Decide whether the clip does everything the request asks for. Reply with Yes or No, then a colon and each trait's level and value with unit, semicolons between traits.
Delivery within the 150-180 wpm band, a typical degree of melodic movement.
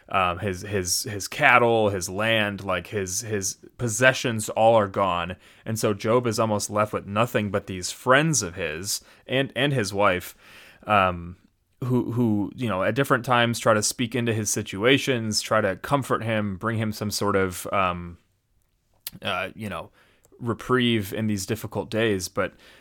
Yes: average, 170 wpm; average, 3.1 semitones